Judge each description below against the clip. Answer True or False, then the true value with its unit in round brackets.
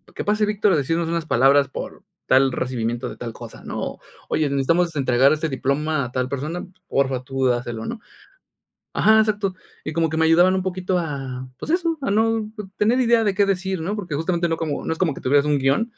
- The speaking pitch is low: False (160 Hz)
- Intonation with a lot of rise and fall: True (6.1 semitones)